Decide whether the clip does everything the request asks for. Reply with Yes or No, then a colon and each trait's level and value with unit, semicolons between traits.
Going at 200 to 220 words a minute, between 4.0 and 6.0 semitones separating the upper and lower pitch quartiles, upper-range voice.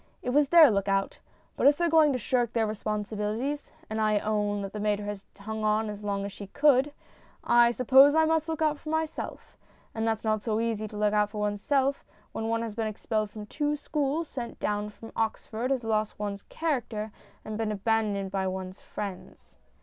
Yes: fast, 205 wpm; average, 4.4 semitones; high, 220 Hz